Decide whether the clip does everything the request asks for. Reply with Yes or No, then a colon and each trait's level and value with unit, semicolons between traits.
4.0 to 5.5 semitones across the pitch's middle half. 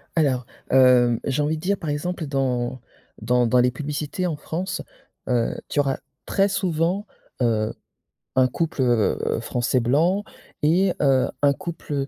Yes: average, 4.9 semitones